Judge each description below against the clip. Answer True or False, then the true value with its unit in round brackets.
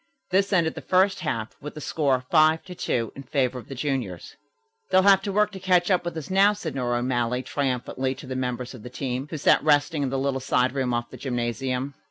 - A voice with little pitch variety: False (5.3 semitones)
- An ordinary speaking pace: False (235 wpm)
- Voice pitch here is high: False (135 Hz)